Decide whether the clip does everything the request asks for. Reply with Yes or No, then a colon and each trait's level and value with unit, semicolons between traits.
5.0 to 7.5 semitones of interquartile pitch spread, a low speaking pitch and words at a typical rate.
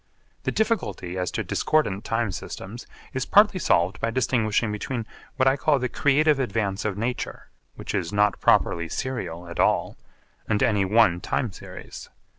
Yes: wide, 5.4 semitones; low, 115 Hz; average, 160 wpm